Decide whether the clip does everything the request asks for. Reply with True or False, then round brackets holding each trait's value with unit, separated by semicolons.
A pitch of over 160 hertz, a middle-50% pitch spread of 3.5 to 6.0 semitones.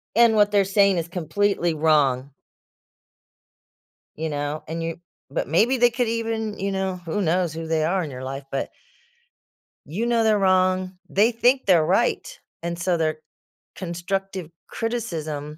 True (185 Hz; 4.6 semitones)